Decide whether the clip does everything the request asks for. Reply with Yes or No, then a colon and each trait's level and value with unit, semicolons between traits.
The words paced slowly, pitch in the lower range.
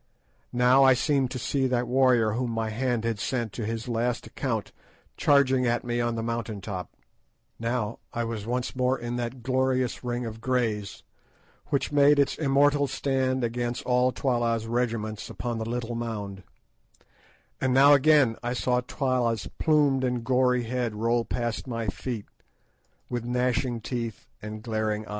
No: average, 160 wpm; low, 120 Hz